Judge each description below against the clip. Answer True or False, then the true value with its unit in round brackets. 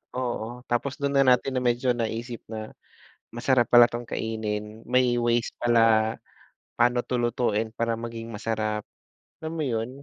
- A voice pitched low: True (120 Hz)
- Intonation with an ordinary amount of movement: False (1.6 semitones)